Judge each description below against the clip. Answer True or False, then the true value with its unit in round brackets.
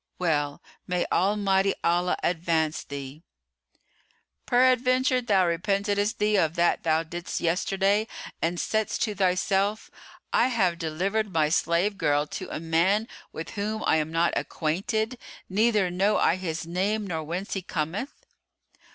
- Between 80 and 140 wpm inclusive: True (135 wpm)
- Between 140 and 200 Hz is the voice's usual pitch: True (185 Hz)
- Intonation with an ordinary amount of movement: True (4.1 semitones)